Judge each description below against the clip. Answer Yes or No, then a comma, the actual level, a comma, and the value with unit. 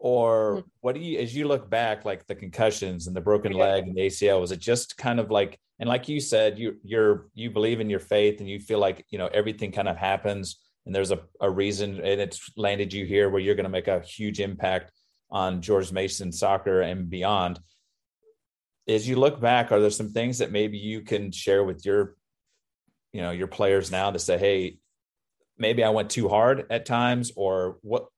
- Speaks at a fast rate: Yes, fast, 215 wpm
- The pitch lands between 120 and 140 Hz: No, low, 100 Hz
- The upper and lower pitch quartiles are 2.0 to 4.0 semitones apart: Yes, average, 2.9 semitones